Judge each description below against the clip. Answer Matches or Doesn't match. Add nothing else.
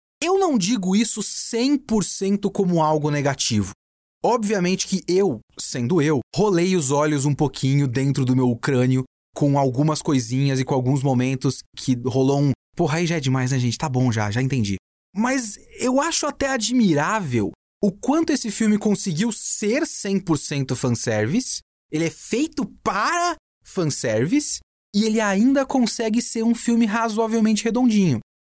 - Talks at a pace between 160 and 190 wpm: Doesn't match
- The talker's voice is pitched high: Doesn't match